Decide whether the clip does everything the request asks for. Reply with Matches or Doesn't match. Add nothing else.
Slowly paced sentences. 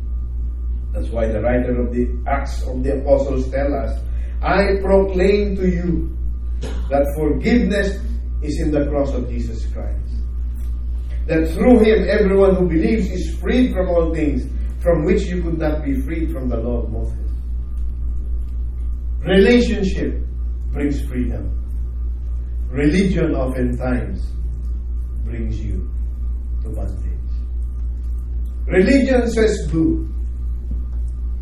Matches